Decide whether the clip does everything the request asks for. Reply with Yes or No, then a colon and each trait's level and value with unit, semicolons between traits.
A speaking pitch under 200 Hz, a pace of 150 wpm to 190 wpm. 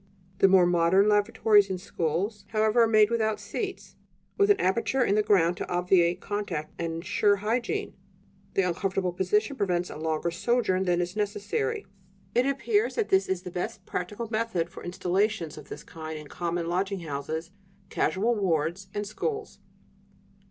Yes: high, 190 Hz; average, 160 wpm